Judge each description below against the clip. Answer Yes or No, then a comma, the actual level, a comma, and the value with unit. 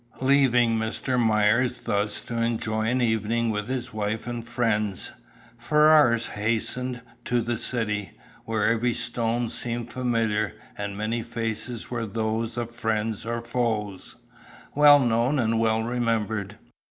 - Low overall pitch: Yes, low, 115 Hz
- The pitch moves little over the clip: Yes, narrow, 1.7 semitones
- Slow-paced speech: Yes, slow, 130 wpm